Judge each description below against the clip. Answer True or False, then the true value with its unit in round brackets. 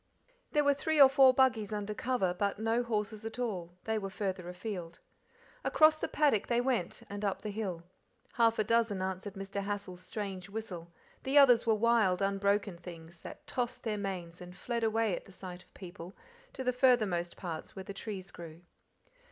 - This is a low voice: False (205 Hz)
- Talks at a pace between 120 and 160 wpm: False (185 wpm)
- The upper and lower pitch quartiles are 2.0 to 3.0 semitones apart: False (4.0 semitones)